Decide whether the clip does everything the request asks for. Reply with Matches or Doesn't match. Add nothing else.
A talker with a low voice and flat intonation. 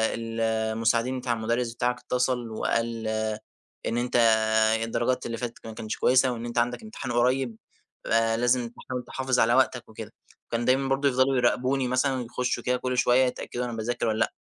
Matches